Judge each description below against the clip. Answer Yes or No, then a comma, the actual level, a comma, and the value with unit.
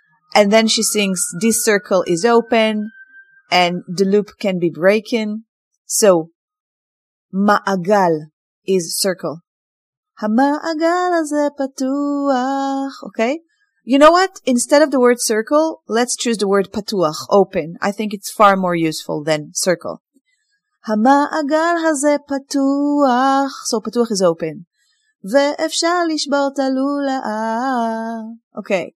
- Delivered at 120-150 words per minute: No, average, 105 wpm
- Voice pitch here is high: Yes, high, 230 Hz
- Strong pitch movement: Yes, wide, 6.1 semitones